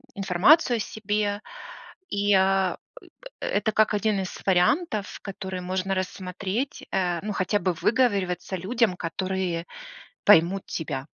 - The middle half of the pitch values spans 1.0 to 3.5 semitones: Yes, narrow, 2.4 semitones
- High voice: Yes, high, 195 Hz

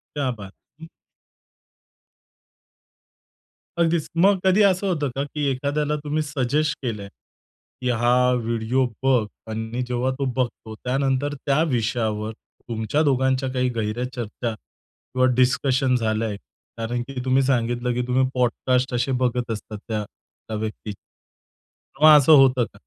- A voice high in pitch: No, low, 125 Hz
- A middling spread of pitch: Yes, average, 3.1 semitones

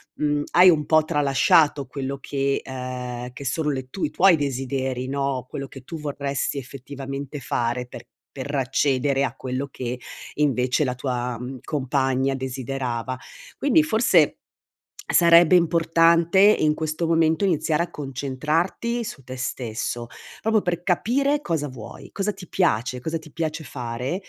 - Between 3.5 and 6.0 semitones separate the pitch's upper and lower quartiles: Yes, average, 4.1 semitones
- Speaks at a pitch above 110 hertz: Yes, medium, 140 Hz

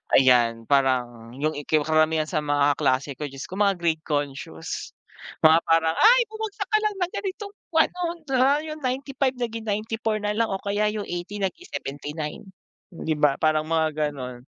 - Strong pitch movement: Yes, wide, 8.7 semitones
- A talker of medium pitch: Yes, medium, 160 Hz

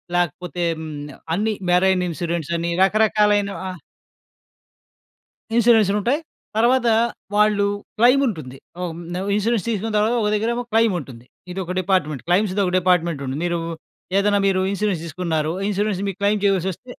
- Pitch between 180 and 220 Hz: Yes, high, 190 Hz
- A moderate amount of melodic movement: Yes, average, 3.6 semitones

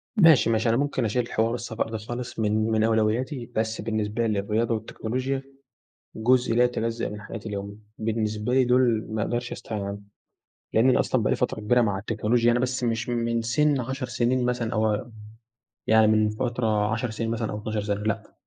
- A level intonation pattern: Yes, narrow, 2.1 semitones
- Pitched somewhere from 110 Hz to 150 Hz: Yes, low, 115 Hz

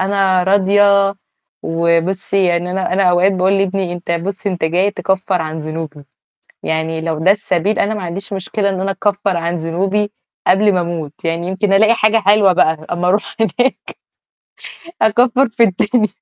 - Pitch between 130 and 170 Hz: No, high, 190 Hz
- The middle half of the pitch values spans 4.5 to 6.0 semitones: No, average, 2.8 semitones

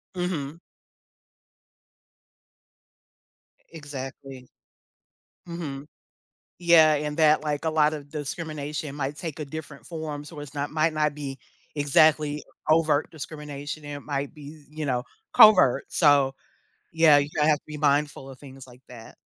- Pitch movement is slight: Yes, narrow, 1.7 semitones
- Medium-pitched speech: Yes, medium, 150 Hz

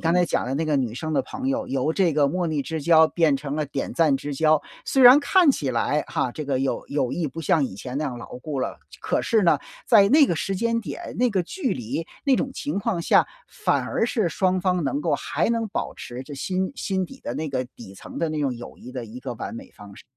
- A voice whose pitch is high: No, medium, 155 Hz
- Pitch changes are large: Yes, wide, 6.3 semitones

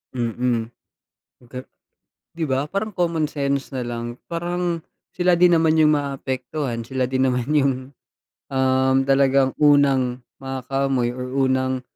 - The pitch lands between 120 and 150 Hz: Yes, low, 135 Hz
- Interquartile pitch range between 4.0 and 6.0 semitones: No, average, 2.9 semitones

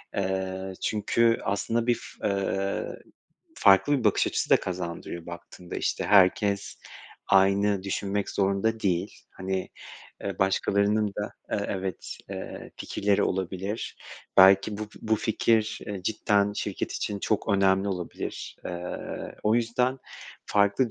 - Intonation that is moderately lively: No, narrow, 1.8 semitones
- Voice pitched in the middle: No, low, 100 Hz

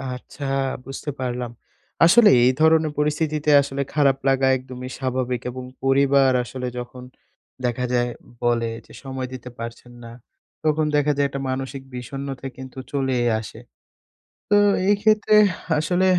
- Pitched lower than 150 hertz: Yes, low, 135 Hz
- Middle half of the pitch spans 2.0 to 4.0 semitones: Yes, average, 2.8 semitones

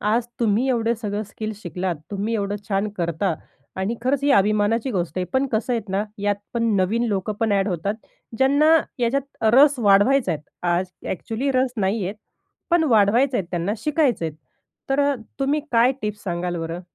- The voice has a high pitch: Yes, high, 215 Hz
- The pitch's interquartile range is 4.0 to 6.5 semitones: Yes, average, 4.7 semitones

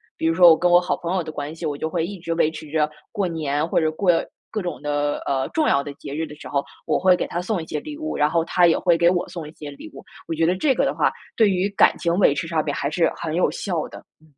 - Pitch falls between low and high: Yes, medium, 165 Hz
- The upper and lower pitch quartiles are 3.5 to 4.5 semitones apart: No, average, 2.9 semitones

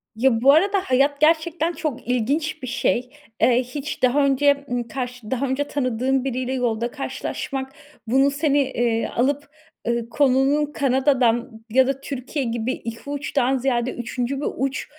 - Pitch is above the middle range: Yes, very high, 265 Hz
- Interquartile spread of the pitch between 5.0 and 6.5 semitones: No, narrow, 2.6 semitones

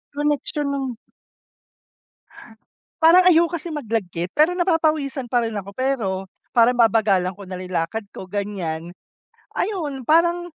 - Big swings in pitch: Yes, wide, 7.8 semitones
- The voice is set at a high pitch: Yes, very high, 250 Hz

